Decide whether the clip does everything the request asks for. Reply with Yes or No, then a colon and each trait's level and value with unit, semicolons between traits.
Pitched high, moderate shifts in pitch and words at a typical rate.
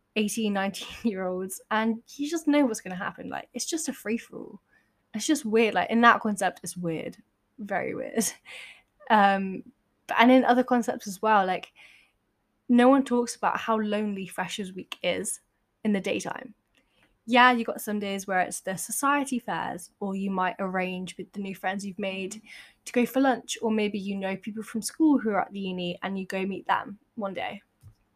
Yes: high, 210 Hz; average, 4.0 semitones; average, 190 wpm